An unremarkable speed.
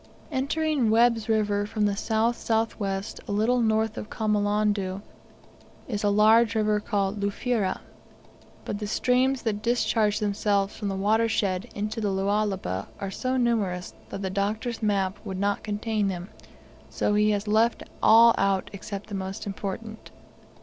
Yes: average, 150 wpm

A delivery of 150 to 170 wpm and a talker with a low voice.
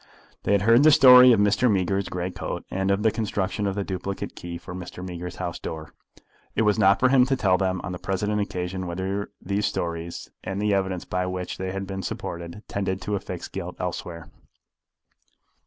No: average, 200 wpm; very low, 95 Hz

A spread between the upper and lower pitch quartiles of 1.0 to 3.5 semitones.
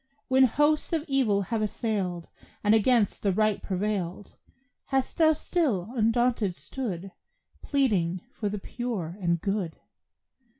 No: average, 5.3 semitones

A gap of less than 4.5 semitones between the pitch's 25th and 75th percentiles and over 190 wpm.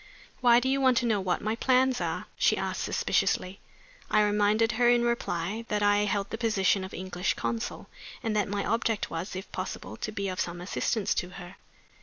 Yes: average, 3.5 semitones; average, 200 wpm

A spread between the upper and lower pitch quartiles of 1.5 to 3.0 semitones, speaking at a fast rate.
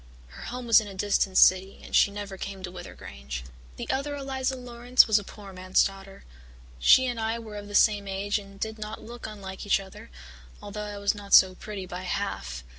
Yes: narrow, 2.6 semitones; fast, 215 wpm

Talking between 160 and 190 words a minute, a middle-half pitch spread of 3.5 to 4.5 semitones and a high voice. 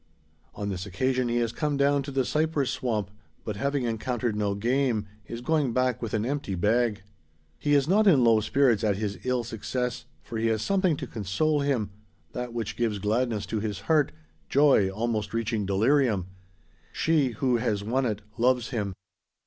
No: average, 180 wpm; average, 4.2 semitones; low, 120 Hz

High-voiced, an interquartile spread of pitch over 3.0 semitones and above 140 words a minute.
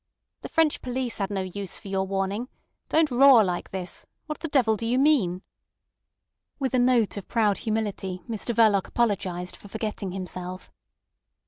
Yes: high, 215 Hz; average, 4.4 semitones; average, 160 wpm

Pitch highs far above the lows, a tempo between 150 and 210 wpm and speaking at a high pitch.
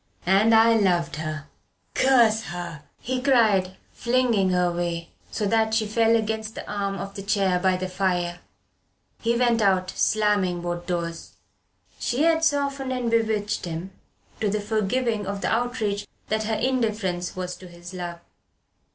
No: average, 4.0 semitones; average, 155 wpm; high, 205 Hz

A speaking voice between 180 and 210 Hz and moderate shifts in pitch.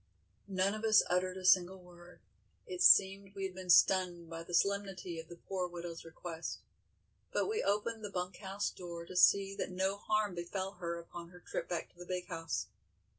No: medium, 185 Hz; narrow, 2.2 semitones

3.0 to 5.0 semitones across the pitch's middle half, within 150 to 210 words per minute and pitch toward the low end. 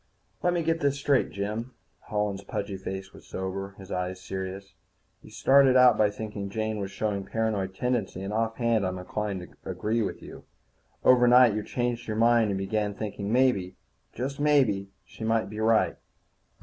Yes: average, 3.6 semitones; average, 175 wpm; low, 105 Hz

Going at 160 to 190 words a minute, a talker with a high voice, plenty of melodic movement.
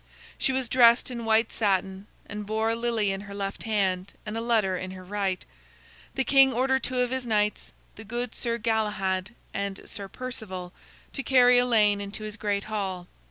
No: average, 185 wpm; high, 215 Hz; average, 3.2 semitones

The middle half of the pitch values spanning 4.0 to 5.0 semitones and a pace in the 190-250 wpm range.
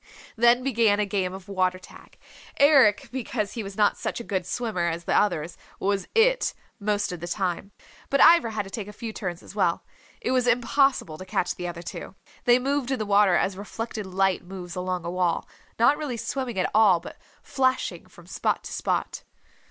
Yes: average, 4.6 semitones; average, 200 wpm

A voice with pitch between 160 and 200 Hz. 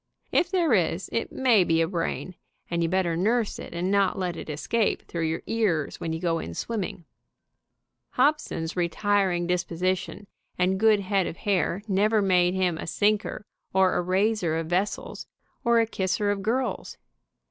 Yes: high, 190 Hz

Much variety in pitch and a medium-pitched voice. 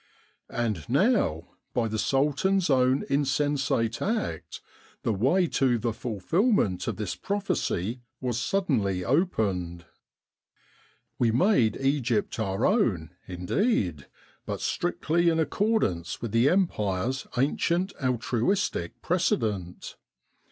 No: wide, 8.8 semitones; low, 125 Hz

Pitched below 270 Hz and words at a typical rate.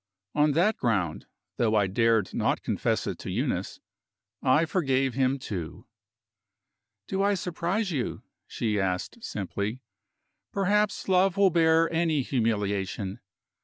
No: low, 135 Hz; slow, 125 wpm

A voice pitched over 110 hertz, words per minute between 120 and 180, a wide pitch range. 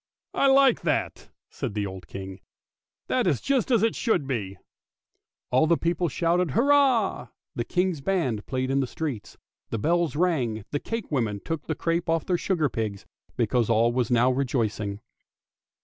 Yes: medium, 140 Hz; average, 175 wpm; wide, 7.5 semitones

